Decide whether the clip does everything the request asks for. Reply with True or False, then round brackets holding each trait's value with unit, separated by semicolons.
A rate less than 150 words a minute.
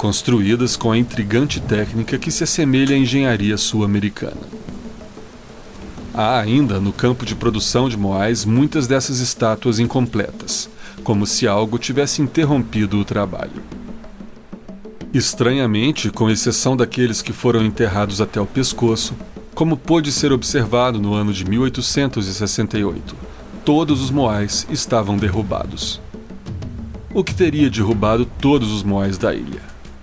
True (125 wpm)